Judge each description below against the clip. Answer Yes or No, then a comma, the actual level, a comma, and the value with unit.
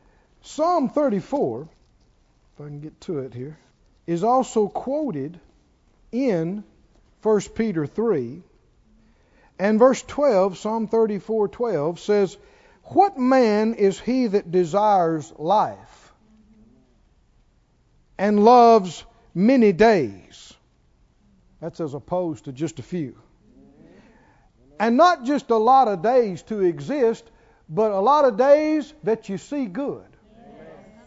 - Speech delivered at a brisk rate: No, slow, 115 wpm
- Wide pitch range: Yes, wide, 6.7 semitones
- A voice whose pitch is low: No, high, 210 Hz